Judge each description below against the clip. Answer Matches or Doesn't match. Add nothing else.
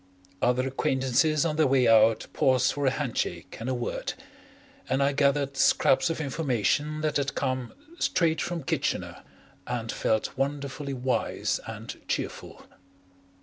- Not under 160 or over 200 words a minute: Doesn't match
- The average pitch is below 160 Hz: Matches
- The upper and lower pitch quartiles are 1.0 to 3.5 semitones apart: Matches